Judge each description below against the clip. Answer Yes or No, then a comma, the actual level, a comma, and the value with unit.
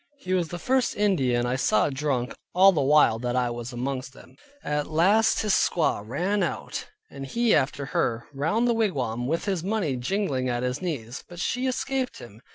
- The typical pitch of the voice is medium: Yes, medium, 150 Hz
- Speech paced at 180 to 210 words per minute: Yes, average, 190 wpm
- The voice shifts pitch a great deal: Yes, wide, 7.6 semitones